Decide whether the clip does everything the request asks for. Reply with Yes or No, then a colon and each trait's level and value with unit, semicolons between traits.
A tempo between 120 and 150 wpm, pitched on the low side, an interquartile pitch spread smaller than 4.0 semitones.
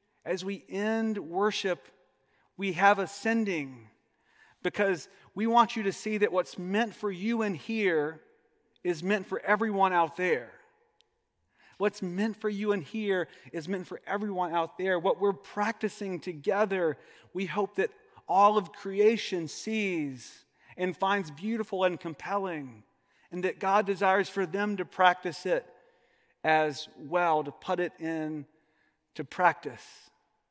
No: average, 140 wpm; high, 195 Hz; average, 2.9 semitones